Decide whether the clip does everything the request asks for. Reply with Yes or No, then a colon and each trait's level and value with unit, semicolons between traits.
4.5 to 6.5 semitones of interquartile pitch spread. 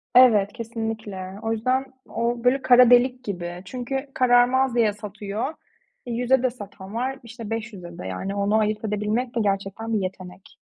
No: average, 3.5 semitones